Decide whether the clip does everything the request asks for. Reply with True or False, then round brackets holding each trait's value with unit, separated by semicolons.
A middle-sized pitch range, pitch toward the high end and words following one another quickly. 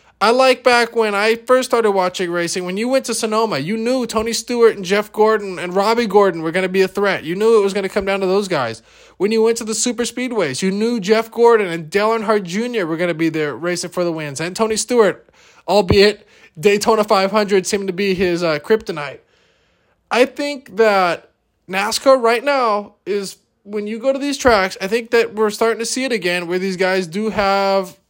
True (3.3 semitones; 210 Hz; 220 wpm)